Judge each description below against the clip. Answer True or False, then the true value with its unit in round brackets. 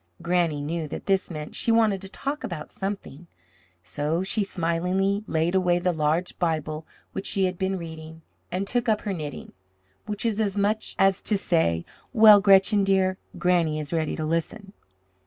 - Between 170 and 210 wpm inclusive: True (175 wpm)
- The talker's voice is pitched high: False (180 Hz)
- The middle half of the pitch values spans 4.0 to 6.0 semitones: False (3.6 semitones)